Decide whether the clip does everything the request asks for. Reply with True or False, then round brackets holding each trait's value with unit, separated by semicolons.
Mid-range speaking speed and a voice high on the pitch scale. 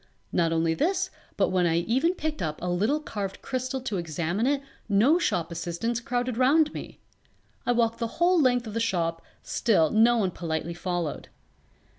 True (175 wpm; 225 Hz)